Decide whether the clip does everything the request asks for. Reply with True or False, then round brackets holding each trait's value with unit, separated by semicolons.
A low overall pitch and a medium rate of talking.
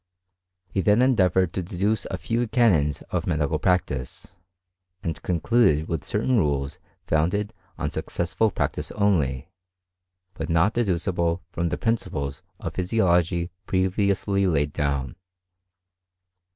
False (90 Hz; 120 wpm)